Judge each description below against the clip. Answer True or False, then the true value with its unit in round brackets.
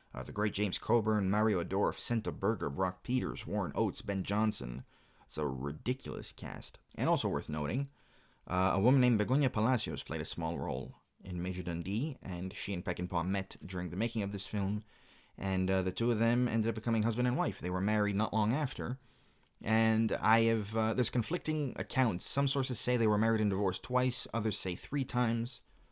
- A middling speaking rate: True (195 wpm)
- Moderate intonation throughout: True (4.6 semitones)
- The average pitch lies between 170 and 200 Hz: False (110 Hz)